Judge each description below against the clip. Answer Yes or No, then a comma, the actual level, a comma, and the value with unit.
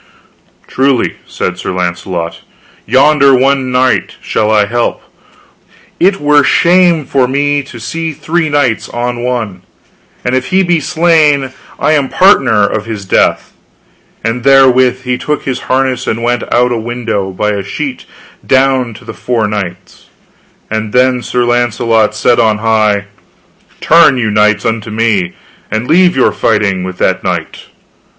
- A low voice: Yes, low, 125 Hz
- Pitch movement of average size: Yes, average, 4.2 semitones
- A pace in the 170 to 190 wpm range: No, average, 155 wpm